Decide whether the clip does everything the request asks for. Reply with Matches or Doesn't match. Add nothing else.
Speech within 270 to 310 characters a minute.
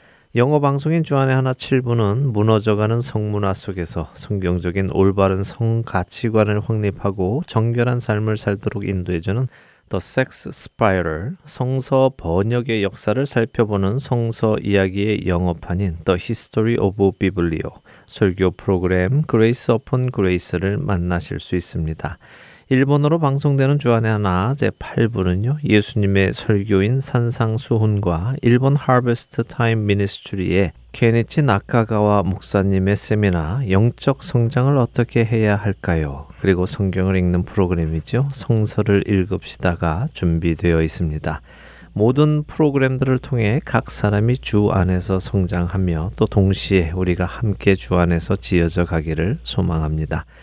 Doesn't match